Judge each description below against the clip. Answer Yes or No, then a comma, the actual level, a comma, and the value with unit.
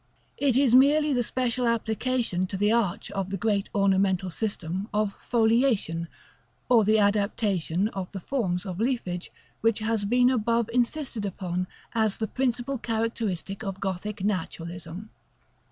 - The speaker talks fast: No, average, 140 wpm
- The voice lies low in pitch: No, high, 215 Hz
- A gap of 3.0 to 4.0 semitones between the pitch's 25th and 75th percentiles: Yes, average, 3.7 semitones